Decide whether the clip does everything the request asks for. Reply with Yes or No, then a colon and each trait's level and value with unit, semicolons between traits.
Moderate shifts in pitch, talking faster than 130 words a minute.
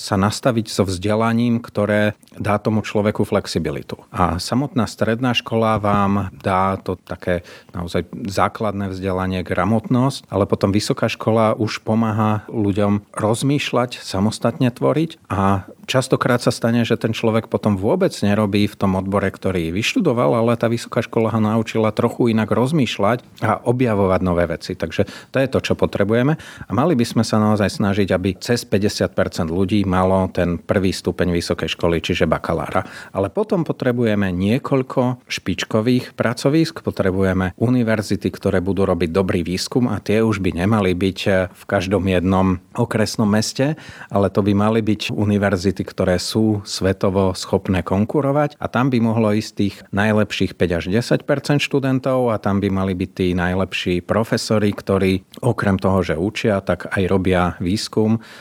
Yes: average, 3.5 semitones; average, 150 wpm